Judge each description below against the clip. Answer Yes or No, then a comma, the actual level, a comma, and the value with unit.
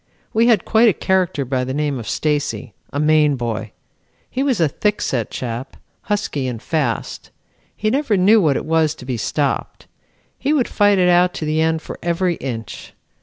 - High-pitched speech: No, medium, 155 Hz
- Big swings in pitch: Yes, wide, 7.1 semitones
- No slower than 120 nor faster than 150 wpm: No, average, 185 wpm